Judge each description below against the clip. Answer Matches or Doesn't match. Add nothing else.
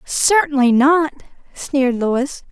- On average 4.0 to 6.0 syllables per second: Doesn't match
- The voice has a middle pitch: Doesn't match